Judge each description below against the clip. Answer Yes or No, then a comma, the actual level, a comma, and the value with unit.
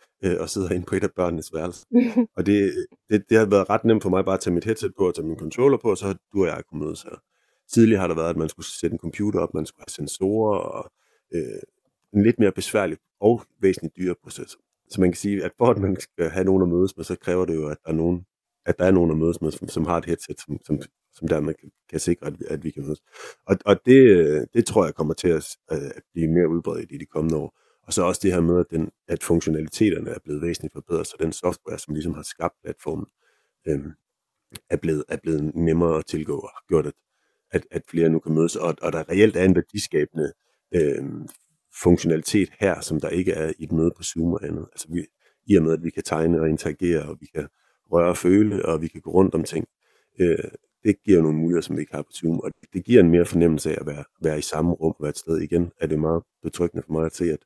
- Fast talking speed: Yes, fast, 260 wpm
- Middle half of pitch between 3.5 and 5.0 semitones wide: No, average, 2.8 semitones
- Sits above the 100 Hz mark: No, very low, 85 Hz